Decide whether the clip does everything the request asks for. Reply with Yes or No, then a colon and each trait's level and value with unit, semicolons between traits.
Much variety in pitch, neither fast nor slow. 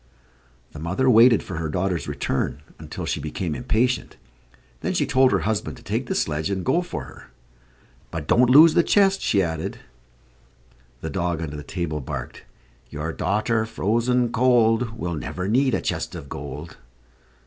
Yes: wide, 7.3 semitones; average, 165 wpm